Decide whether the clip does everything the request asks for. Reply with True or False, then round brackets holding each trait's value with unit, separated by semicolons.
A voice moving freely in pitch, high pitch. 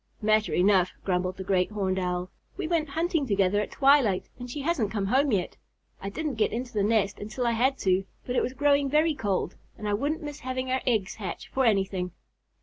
True (5.9 semitones; 220 Hz)